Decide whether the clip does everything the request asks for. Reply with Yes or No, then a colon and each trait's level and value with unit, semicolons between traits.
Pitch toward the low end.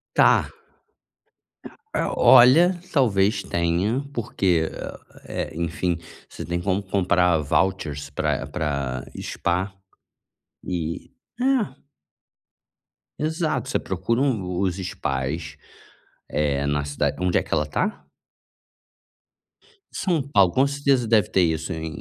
Yes: very low, 90 Hz